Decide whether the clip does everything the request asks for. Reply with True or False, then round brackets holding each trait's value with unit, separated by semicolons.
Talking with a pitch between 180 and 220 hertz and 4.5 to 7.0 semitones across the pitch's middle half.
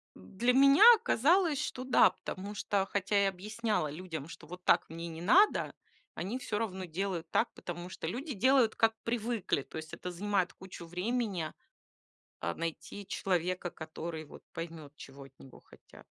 True (185 Hz; 5.2 semitones)